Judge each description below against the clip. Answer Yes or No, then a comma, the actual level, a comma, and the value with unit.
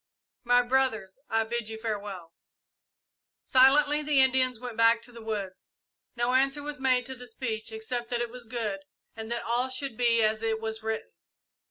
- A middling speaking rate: Yes, average, 180 wpm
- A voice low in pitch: No, high, 235 Hz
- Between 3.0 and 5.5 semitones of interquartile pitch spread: No, narrow, 2.6 semitones